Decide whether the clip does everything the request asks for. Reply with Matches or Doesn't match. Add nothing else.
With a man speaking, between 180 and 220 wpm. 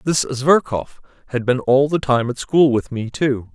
Matches